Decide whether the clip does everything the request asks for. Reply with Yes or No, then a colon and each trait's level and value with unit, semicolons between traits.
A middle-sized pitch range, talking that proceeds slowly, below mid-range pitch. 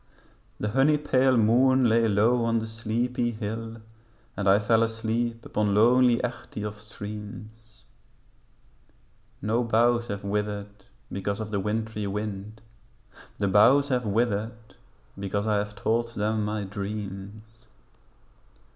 No: narrow, 2.0 semitones; slow, 125 wpm; low, 110 Hz